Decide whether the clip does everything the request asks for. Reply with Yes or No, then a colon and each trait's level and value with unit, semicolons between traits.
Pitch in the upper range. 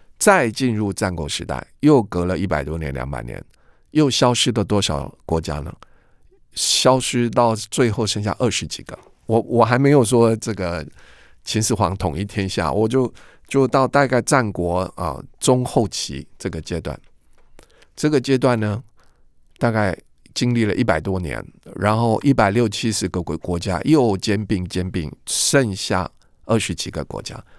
No: low, 105 Hz